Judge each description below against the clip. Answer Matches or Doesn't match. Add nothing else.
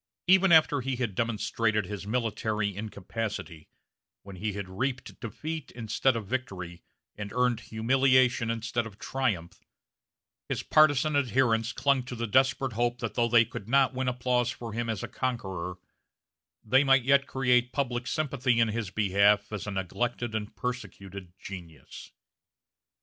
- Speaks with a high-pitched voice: Doesn't match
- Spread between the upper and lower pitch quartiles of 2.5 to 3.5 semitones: Doesn't match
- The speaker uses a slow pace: Doesn't match